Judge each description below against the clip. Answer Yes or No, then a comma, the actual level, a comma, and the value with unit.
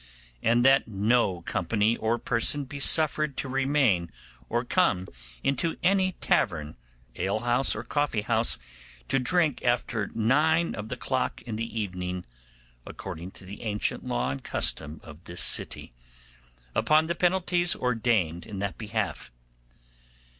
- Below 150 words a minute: Yes, average, 140 wpm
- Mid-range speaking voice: No, low, 115 Hz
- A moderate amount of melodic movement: No, wide, 6.0 semitones